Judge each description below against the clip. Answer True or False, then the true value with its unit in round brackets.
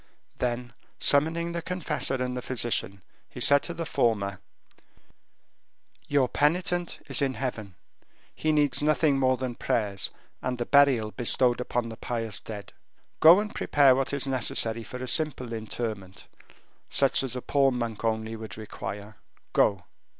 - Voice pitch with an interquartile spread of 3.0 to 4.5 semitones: True (4.1 semitones)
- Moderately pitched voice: False (125 Hz)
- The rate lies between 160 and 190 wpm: False (150 wpm)